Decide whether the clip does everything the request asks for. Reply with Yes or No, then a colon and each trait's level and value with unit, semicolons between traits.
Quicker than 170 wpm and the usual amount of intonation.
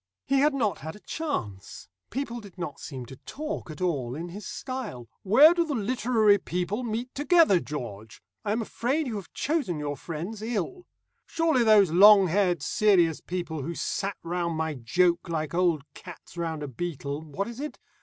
No: average, 180 wpm; wide, 6.9 semitones